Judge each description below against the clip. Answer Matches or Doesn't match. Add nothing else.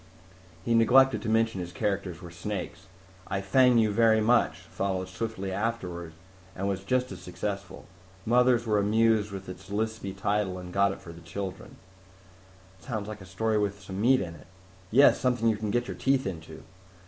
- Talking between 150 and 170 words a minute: Doesn't match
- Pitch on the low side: Matches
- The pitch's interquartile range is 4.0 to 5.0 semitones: Doesn't match